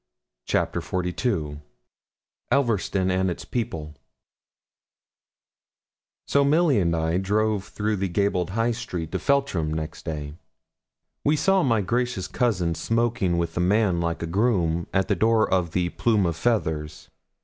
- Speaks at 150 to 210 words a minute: No, average, 140 wpm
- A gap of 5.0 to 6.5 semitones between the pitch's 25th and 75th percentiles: Yes, wide, 5.4 semitones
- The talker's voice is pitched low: Yes, very low, 95 Hz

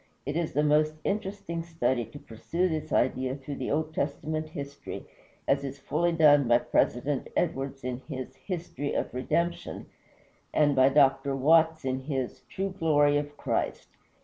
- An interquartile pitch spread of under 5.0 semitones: Yes, average, 3.1 semitones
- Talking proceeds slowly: No, average, 155 wpm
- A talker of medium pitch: Yes, medium, 145 Hz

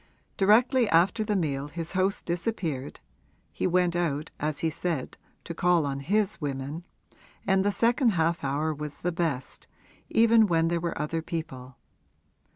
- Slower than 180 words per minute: Yes, average, 155 wpm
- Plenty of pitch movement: No, average, 4.4 semitones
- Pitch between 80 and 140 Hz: No, medium, 170 Hz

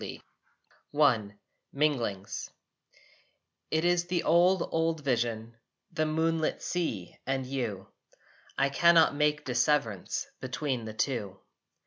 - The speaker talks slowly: Yes, slow, 100 wpm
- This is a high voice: No, medium, 140 Hz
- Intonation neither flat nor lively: No, wide, 5.7 semitones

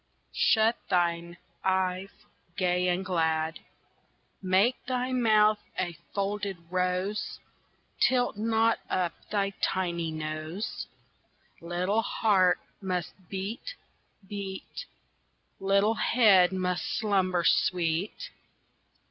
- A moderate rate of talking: No, slow, 90 wpm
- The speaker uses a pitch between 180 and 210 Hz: Yes, high, 190 Hz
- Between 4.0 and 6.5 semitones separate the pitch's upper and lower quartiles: No, average, 3.0 semitones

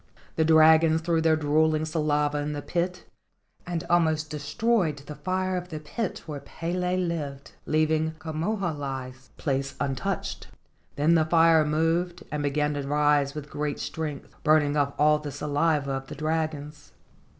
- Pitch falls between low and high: Yes, medium, 155 Hz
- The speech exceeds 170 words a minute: No, average, 160 wpm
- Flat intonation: Yes, narrow, 2.0 semitones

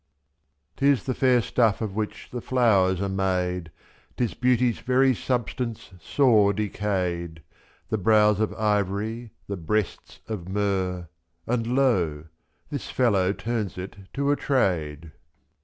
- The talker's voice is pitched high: No, low, 105 Hz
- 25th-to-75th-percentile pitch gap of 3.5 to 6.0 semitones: Yes, average, 4.6 semitones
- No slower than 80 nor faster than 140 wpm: Yes, slow, 135 wpm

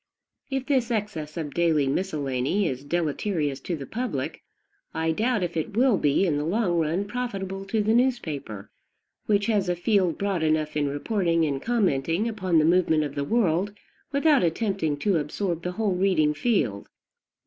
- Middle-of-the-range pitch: Yes, medium, 175 Hz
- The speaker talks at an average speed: Yes, average, 170 wpm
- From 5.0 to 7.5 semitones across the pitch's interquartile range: Yes, wide, 5.5 semitones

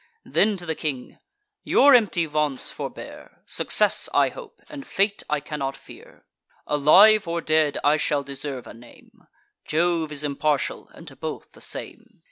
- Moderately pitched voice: Yes, medium, 155 Hz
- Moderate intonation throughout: Yes, average, 3.5 semitones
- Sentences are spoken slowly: No, average, 155 wpm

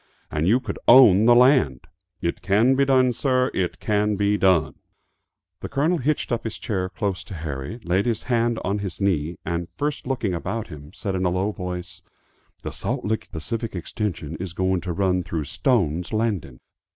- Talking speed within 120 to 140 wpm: No, average, 185 wpm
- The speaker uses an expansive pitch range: No, average, 4.8 semitones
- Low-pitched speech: Yes, low, 100 Hz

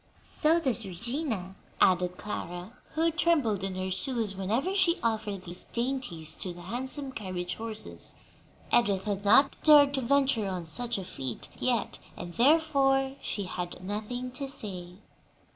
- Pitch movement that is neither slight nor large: No, wide, 6.4 semitones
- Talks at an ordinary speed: Yes, average, 145 wpm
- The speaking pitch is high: Yes, high, 220 Hz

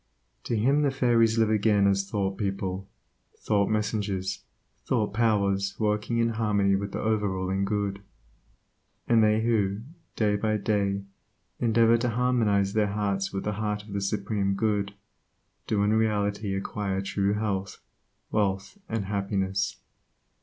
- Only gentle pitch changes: Yes, narrow, 1.9 semitones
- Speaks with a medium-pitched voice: No, low, 105 Hz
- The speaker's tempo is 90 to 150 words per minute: Yes, average, 140 wpm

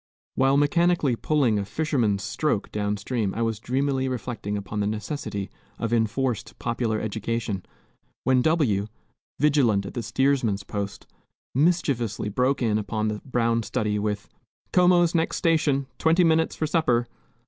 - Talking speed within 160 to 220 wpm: No, average, 140 wpm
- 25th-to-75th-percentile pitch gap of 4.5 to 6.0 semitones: Yes, average, 5.3 semitones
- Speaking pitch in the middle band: No, low, 120 Hz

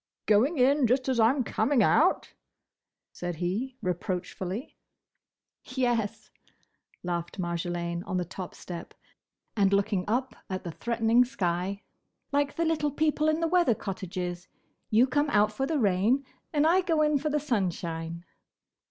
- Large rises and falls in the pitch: Yes, wide, 7.5 semitones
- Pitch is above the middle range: Yes, high, 220 Hz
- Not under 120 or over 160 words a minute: Yes, average, 145 wpm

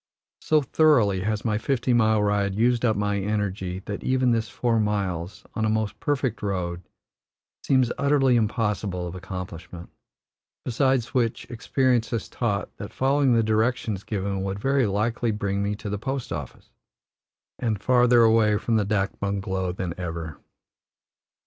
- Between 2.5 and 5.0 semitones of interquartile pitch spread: Yes, average, 3.6 semitones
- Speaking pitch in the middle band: No, low, 110 Hz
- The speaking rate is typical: Yes, average, 150 wpm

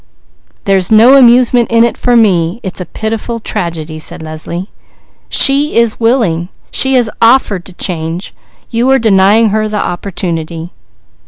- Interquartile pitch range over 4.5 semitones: Yes, average, 5.2 semitones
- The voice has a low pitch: No, high, 215 Hz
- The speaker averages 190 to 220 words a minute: No, average, 145 wpm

